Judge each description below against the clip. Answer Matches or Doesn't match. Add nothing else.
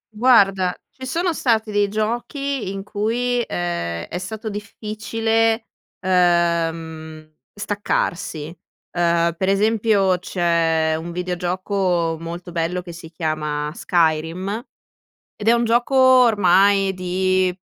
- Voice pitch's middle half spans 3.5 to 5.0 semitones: Matches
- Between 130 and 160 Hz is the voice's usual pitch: Doesn't match